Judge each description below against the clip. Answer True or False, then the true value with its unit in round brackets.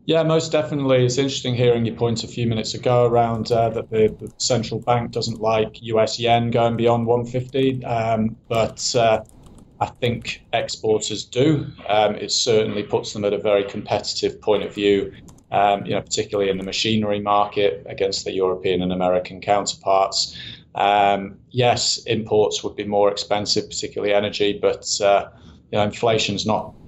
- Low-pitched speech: True (110 Hz)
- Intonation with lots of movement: False (2.8 semitones)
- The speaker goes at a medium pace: True (175 wpm)